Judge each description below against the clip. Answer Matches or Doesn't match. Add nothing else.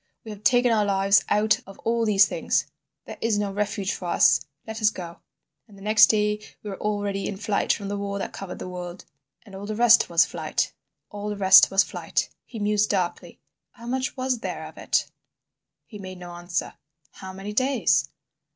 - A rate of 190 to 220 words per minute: Matches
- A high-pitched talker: Matches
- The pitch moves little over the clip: Matches